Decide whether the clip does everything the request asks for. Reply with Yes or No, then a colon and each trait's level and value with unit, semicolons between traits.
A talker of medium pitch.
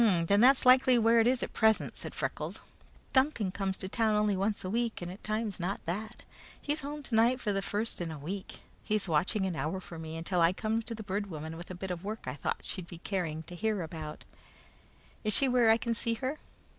No: high, 205 Hz